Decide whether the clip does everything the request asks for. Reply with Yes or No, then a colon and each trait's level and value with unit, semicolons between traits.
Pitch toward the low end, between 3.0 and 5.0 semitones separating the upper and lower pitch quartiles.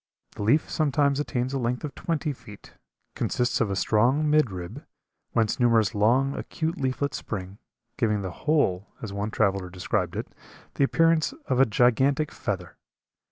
No: low, 120 Hz; wide, 5.5 semitones